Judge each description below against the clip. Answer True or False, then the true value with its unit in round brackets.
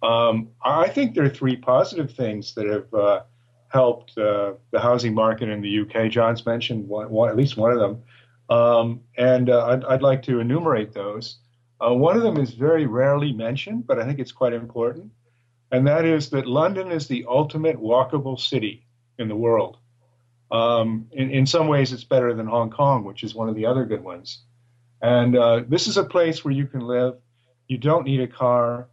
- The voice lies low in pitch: True (120 Hz)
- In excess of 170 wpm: True (200 wpm)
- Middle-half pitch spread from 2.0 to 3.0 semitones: True (2.6 semitones)